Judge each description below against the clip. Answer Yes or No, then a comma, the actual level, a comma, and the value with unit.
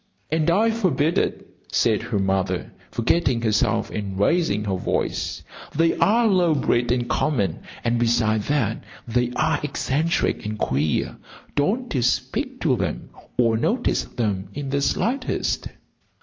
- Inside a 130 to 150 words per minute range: Yes, average, 140 wpm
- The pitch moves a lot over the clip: Yes, wide, 7.1 semitones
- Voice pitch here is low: Yes, low, 125 Hz